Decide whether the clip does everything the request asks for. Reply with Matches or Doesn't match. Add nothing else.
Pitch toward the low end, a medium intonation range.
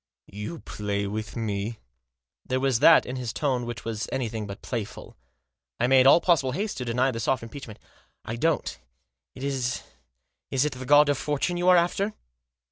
Matches